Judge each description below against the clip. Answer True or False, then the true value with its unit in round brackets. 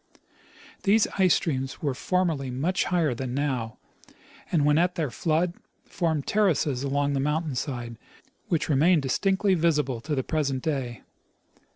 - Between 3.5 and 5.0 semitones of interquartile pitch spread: True (4.2 semitones)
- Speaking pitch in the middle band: True (150 Hz)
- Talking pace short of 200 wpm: True (145 wpm)